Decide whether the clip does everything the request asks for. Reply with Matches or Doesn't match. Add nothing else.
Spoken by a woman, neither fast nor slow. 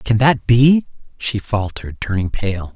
Doesn't match